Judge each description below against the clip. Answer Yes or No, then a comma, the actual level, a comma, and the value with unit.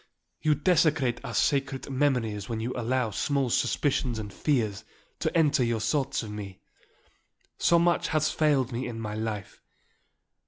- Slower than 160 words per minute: Yes, average, 150 wpm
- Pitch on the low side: Yes, low, 125 Hz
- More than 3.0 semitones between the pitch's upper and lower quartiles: Yes, average, 4.5 semitones